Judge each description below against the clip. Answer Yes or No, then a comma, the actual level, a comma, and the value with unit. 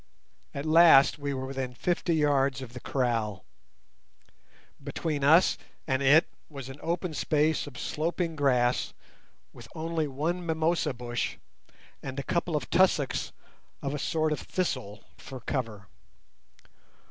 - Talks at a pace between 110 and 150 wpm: Yes, slow, 135 wpm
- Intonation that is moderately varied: Yes, average, 3.6 semitones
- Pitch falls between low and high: Yes, medium, 145 Hz